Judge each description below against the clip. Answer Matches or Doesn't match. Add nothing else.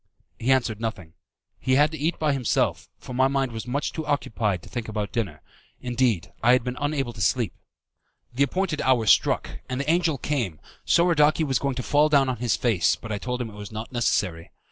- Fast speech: Matches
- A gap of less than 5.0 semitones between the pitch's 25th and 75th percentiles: Matches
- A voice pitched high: Doesn't match